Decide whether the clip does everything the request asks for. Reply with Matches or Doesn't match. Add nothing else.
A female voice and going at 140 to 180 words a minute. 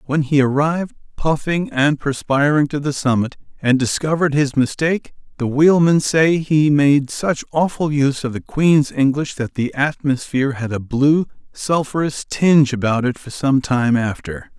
Doesn't match